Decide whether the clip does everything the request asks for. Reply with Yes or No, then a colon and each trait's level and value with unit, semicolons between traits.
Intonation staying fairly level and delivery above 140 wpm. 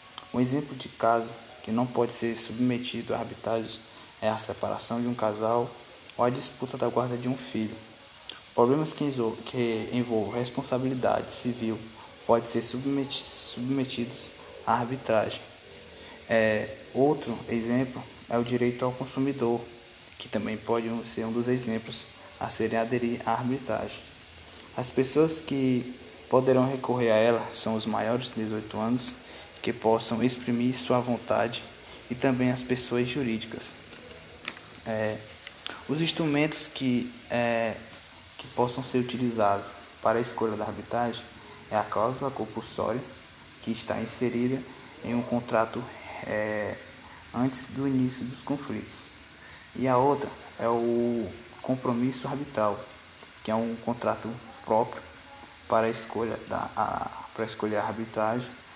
No: narrow, 2.0 semitones; average, 130 wpm